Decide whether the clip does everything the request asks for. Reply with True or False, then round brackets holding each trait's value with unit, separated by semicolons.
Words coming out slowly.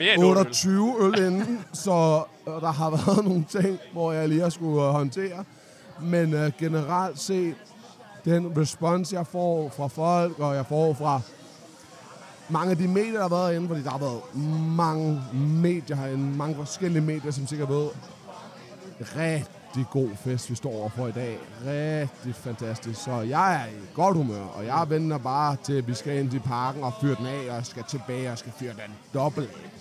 False (180 wpm)